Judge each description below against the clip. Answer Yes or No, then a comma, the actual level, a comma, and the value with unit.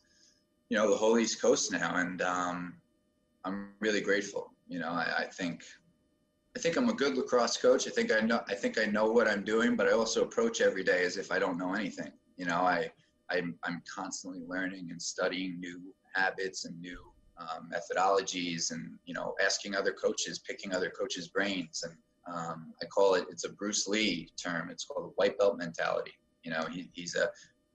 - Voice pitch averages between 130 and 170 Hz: No, low, 105 Hz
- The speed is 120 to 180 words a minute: No, average, 200 wpm